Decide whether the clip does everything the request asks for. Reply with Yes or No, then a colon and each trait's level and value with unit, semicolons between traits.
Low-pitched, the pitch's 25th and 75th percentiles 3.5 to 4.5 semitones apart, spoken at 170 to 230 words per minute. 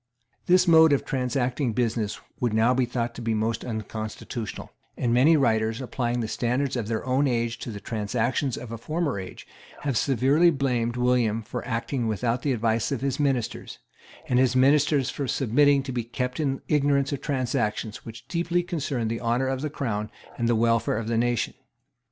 No: low, 125 Hz; average, 3.1 semitones; average, 180 wpm